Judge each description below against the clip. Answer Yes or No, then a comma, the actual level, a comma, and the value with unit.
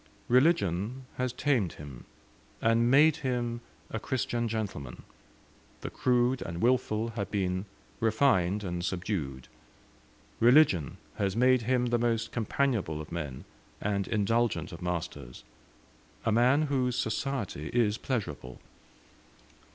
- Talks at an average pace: No, slow, 115 wpm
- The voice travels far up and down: Yes, wide, 5.7 semitones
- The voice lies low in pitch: Yes, low, 115 Hz